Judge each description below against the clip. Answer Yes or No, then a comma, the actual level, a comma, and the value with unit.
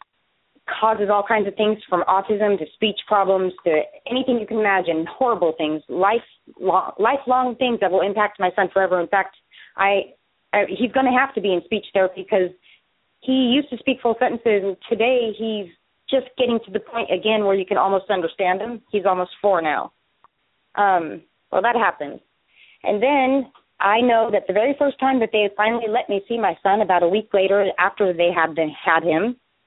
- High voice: Yes, high, 205 Hz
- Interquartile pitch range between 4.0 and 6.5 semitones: No, average, 3.6 semitones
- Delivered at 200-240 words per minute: No, average, 190 wpm